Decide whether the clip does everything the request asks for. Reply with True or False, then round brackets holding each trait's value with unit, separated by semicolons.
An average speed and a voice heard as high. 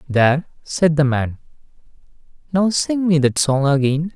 False (145 wpm; 150 Hz)